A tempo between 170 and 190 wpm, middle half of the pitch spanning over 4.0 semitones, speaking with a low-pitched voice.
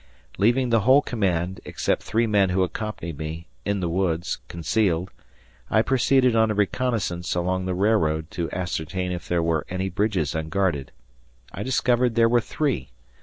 No: average, 160 wpm; average, 4.7 semitones; very low, 95 Hz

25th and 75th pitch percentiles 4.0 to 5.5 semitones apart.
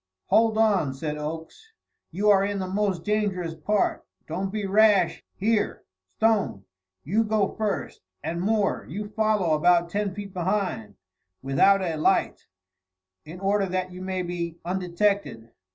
No: average, 3.5 semitones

